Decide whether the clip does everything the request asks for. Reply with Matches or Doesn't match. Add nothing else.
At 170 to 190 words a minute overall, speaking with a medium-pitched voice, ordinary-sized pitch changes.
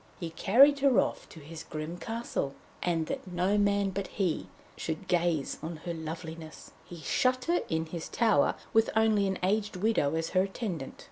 Matches